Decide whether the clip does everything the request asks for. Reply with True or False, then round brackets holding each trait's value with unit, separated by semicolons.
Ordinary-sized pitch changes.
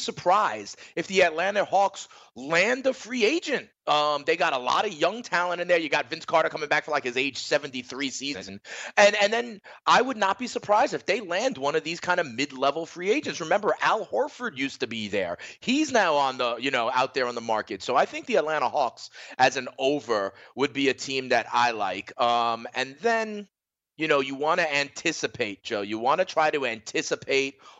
False (6.8 semitones)